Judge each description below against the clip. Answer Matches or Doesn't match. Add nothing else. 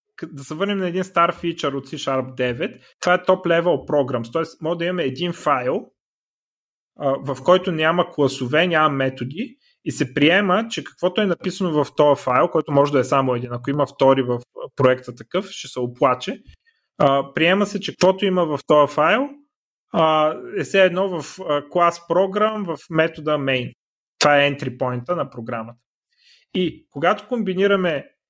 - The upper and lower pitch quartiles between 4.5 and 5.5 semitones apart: Matches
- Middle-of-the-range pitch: Matches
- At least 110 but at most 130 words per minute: Doesn't match